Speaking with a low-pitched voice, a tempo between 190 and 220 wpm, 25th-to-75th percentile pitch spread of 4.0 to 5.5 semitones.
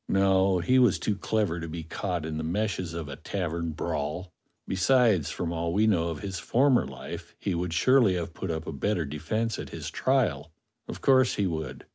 Yes: very low, 90 Hz; average, 200 wpm; average, 4.3 semitones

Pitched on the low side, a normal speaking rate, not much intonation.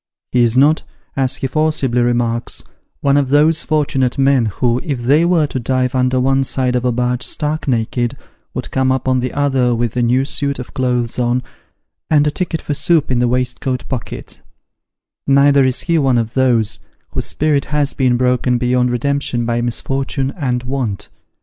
Yes: low, 130 Hz; average, 190 wpm; narrow, 2.3 semitones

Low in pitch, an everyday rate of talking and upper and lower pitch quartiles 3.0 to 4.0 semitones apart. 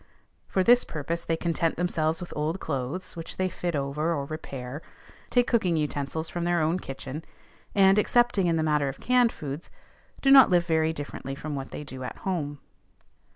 No: medium, 160 Hz; average, 185 wpm; average, 3.6 semitones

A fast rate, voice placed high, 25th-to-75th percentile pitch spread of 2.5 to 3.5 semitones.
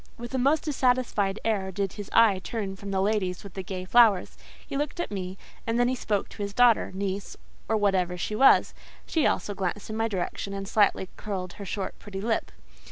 Yes: fast, 210 wpm; high, 205 Hz; average, 3.0 semitones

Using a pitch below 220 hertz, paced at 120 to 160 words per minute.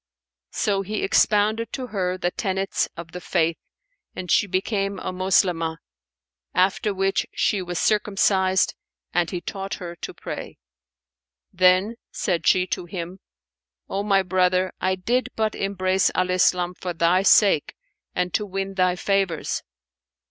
Yes: medium, 185 Hz; average, 140 wpm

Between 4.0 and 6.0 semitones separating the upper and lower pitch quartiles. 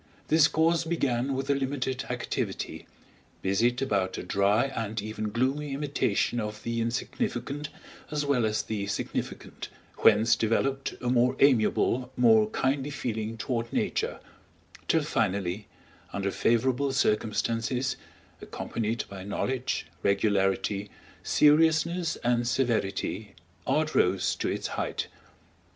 Yes: average, 4.3 semitones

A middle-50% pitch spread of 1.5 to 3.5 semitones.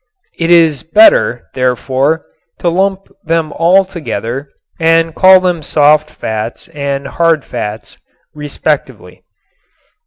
No: average, 4.0 semitones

